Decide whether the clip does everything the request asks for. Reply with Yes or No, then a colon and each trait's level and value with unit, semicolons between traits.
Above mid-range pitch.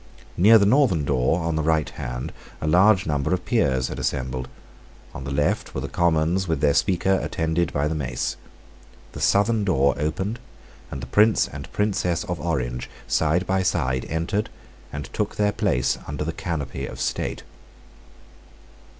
No: very low, 80 Hz